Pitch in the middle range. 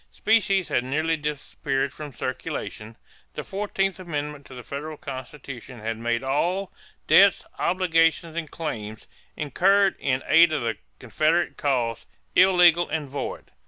Yes: medium, 150 Hz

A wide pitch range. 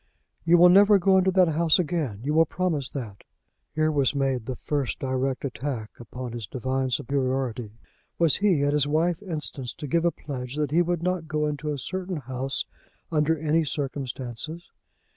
No: average, 4.3 semitones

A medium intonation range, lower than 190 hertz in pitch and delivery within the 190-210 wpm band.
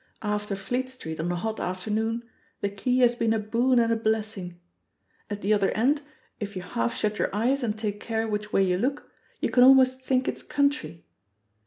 No: average, 3.6 semitones; high, 220 Hz; average, 200 wpm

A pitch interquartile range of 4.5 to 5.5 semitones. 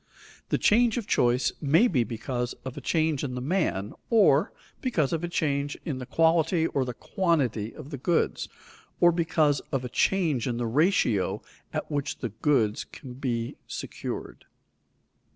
Yes: average, 5.0 semitones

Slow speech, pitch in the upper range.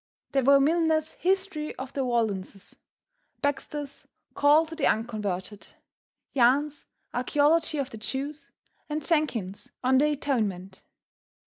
Yes: slow, 115 wpm; very high, 280 Hz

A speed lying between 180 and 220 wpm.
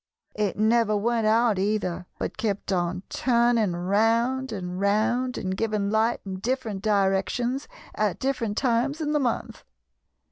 No: average, 140 wpm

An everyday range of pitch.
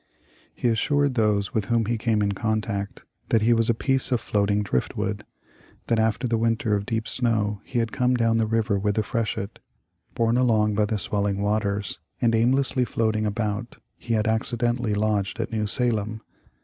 No: narrow, 2.1 semitones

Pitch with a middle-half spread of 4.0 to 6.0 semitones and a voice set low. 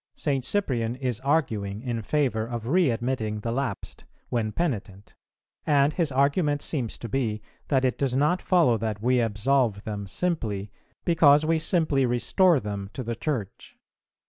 Yes: average, 4.8 semitones; low, 125 Hz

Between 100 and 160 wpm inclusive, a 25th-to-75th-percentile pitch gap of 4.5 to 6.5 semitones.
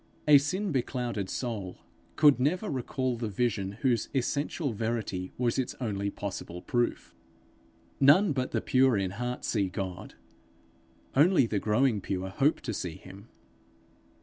Yes: average, 140 wpm; average, 5.2 semitones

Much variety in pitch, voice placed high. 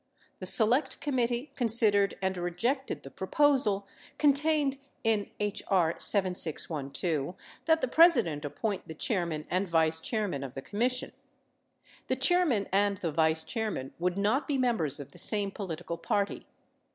Yes: wide, 6.8 semitones; high, 200 Hz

